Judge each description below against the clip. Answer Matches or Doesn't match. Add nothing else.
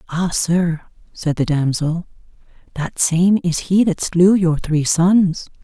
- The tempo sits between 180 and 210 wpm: Doesn't match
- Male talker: Doesn't match